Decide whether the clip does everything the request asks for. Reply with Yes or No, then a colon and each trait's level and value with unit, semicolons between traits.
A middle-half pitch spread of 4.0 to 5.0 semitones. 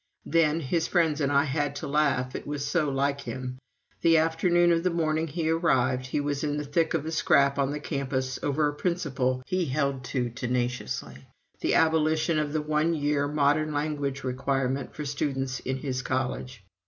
No: average, 2.9 semitones